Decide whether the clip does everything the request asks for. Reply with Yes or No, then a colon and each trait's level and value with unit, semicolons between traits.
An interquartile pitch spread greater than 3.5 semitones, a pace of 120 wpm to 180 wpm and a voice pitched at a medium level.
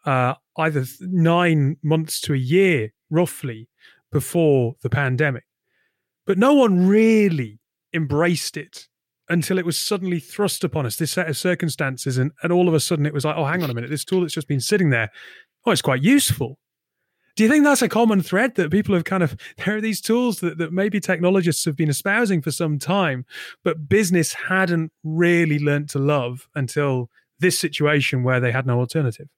No: average, 4.6 semitones; average, 195 wpm; medium, 165 Hz